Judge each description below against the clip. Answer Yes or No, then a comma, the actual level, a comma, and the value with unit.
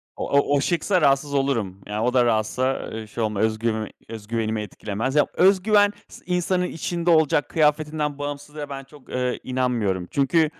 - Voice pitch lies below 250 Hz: Yes, low, 135 Hz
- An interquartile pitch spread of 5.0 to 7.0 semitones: Yes, wide, 5.5 semitones